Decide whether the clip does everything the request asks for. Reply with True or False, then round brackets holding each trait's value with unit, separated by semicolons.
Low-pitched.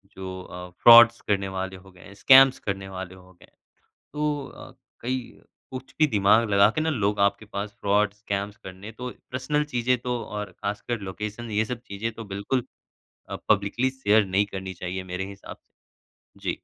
True (105 Hz)